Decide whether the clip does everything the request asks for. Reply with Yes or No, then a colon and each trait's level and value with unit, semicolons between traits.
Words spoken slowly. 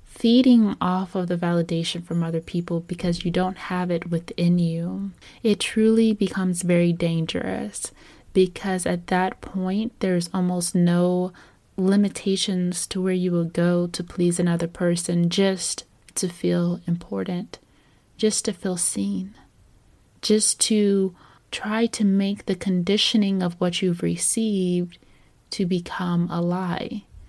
Yes: slow, 130 wpm